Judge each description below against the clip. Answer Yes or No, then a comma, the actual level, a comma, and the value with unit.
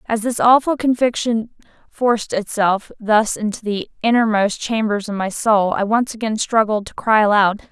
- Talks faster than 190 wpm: No, average, 165 wpm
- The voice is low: No, high, 220 Hz